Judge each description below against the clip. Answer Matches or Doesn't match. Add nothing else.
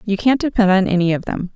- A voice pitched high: Matches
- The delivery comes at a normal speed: Doesn't match